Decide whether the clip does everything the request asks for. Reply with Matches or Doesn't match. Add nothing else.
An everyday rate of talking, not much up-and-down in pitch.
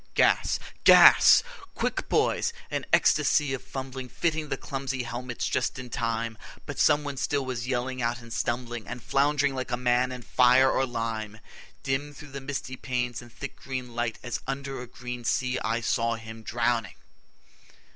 Matches